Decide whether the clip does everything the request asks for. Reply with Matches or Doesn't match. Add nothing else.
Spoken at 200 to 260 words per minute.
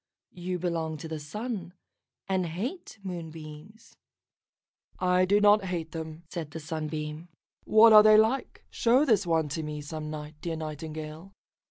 Doesn't match